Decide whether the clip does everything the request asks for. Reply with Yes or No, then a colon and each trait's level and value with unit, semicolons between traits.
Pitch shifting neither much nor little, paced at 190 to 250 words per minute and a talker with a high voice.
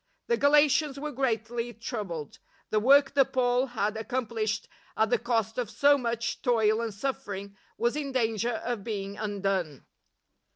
No: average, 3.5 semitones; average, 150 wpm; high, 235 Hz